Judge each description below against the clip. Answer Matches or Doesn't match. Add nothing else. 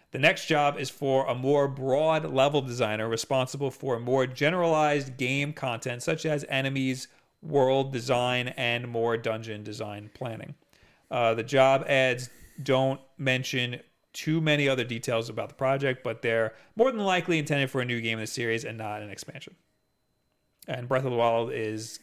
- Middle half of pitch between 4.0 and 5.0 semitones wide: Doesn't match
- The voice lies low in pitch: Matches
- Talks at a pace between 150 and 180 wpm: Matches